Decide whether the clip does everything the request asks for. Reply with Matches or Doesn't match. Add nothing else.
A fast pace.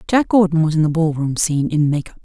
Matches